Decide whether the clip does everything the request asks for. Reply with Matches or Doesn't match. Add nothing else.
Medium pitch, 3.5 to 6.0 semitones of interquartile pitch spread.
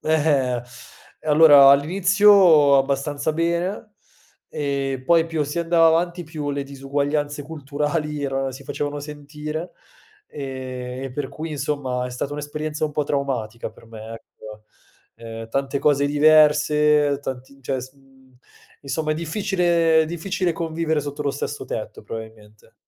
Doesn't match